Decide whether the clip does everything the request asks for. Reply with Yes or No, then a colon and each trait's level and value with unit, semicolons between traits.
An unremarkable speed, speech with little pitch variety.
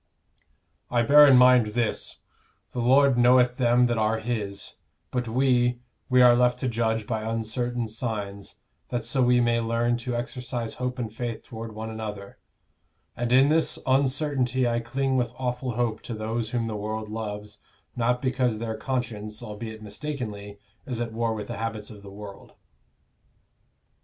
Yes: average, 160 wpm; narrow, 2.2 semitones